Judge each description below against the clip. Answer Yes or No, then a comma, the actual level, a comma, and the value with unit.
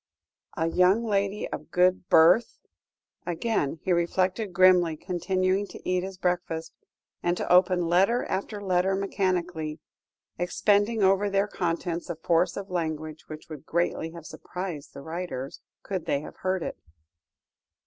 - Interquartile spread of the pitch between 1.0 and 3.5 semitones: Yes, narrow, 2.5 semitones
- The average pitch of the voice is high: No, medium, 180 Hz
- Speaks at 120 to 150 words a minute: Yes, average, 140 wpm